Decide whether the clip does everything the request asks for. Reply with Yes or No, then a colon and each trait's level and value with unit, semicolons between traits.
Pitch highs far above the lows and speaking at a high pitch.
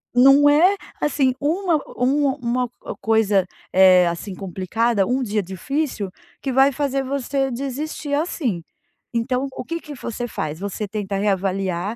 Yes: wide, 6.2 semitones; high, 245 Hz